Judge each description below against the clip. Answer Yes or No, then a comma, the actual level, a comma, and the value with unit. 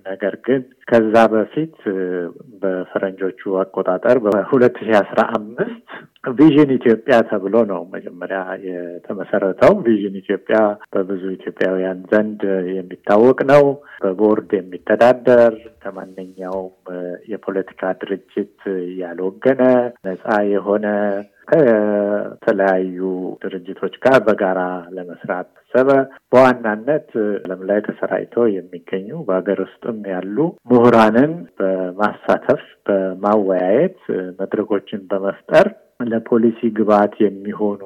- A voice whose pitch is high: No, low, 100 Hz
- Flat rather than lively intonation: No, average, 3.3 semitones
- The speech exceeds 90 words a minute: No, average, 80 wpm